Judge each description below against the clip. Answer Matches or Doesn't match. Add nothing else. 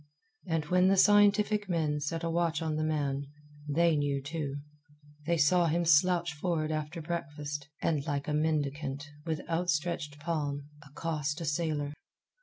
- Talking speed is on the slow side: Doesn't match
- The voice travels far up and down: Doesn't match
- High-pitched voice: Doesn't match